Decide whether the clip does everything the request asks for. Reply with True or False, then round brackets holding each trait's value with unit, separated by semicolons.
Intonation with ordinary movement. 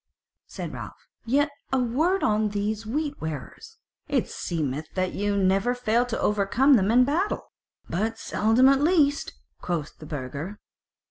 False (6.0 semitones)